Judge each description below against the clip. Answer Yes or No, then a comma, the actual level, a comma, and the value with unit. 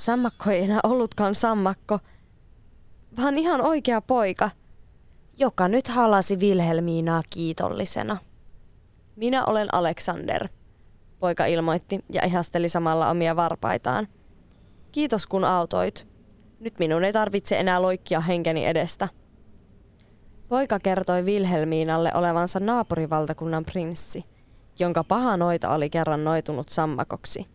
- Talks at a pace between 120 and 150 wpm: No, average, 105 wpm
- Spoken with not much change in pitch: No, average, 4.3 semitones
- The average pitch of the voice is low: No, medium, 175 Hz